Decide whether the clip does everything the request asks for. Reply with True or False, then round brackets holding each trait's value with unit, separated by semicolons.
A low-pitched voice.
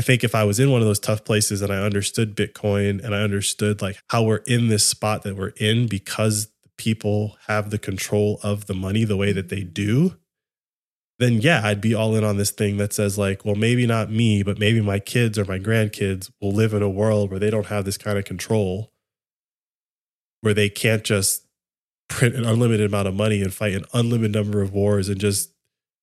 True (105 Hz)